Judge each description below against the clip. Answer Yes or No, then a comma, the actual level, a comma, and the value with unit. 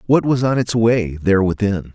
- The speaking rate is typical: No, fast, 215 wpm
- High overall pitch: No, low, 105 Hz